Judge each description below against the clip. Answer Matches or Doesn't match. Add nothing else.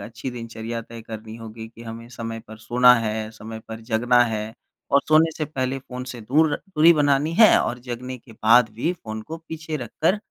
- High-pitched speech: Doesn't match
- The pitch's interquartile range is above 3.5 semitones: Matches